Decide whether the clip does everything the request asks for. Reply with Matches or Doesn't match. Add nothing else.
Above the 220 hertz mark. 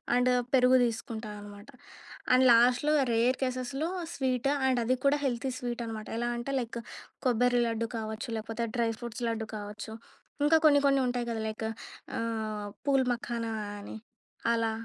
Matches